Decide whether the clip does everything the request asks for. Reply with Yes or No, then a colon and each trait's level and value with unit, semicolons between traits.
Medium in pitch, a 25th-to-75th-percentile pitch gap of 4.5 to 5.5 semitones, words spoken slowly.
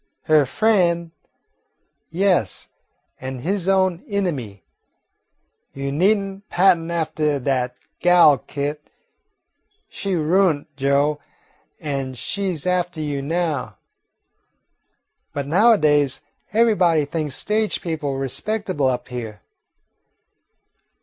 Yes: medium, 155 Hz; average, 5.0 semitones; slow, 95 wpm